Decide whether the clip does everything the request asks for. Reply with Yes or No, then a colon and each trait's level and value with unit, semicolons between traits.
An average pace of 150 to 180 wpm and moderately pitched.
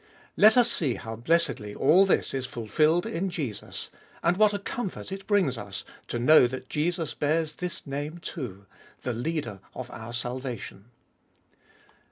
Yes: average, 155 wpm; medium, 150 Hz